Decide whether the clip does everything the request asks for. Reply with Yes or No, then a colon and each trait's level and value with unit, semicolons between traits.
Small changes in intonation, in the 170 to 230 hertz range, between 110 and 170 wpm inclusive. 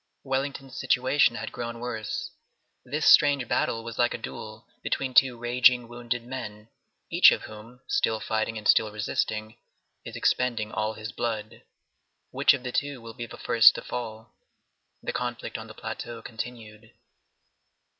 No: narrow, 2.2 semitones; low, 120 Hz; average, 155 wpm